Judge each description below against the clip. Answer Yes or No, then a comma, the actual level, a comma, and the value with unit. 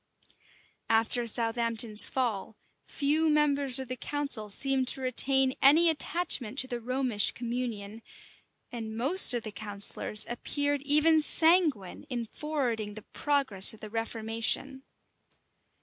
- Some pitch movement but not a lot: Yes, average, 4.2 semitones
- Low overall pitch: No, very high, 250 Hz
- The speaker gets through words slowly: Yes, slow, 120 wpm